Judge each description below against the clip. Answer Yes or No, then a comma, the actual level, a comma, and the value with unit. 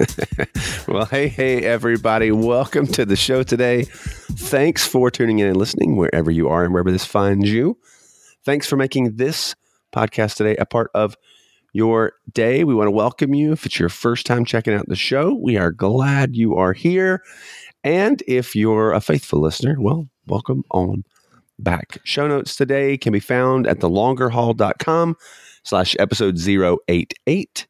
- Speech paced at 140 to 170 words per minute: Yes, average, 165 wpm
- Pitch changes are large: No, average, 4.7 semitones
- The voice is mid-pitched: No, low, 115 Hz